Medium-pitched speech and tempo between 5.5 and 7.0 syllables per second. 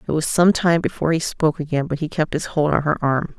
Yes: medium, 155 Hz; 6.2 syllables/s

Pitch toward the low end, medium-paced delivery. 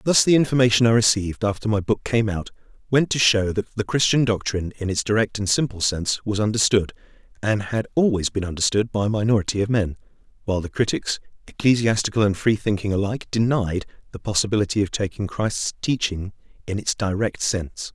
Yes: low, 105 Hz; average, 175 wpm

